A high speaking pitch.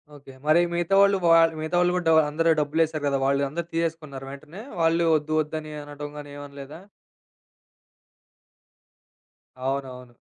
No: medium, 155 Hz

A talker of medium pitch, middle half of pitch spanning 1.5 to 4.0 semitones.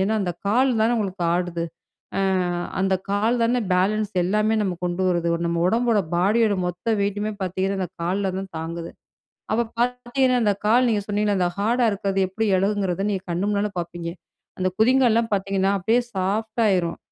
No: high, 200 Hz; average, 3.3 semitones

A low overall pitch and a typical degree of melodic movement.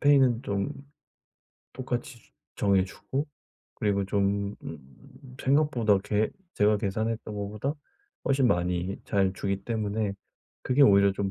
Yes: low, 105 Hz; average, 3.5 semitones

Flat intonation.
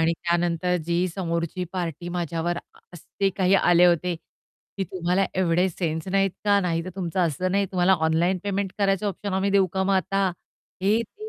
Yes: narrow, 2.3 semitones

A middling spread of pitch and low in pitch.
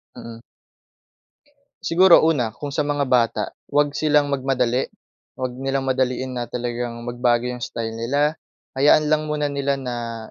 Yes: average, 3.2 semitones; low, 130 Hz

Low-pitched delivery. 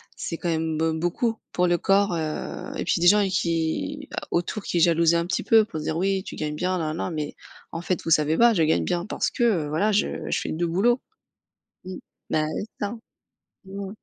No: medium, 175 Hz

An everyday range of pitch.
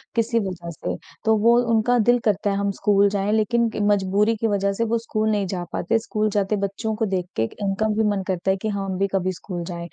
No: narrow, 2.2 semitones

